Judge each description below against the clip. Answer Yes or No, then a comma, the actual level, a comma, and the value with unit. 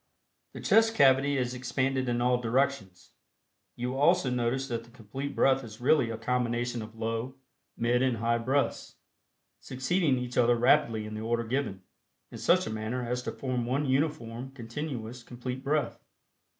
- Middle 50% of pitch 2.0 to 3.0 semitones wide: Yes, narrow, 2.4 semitones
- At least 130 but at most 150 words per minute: No, average, 165 wpm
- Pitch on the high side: No, low, 125 Hz